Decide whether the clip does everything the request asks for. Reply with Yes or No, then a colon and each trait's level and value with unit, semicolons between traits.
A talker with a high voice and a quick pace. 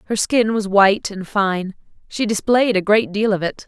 Yes: high, 205 Hz; fast, 210 wpm